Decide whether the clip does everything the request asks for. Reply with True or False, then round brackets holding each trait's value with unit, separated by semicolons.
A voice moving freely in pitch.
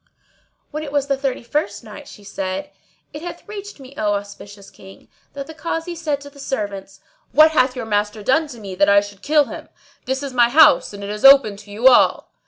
True (6.1 semitones)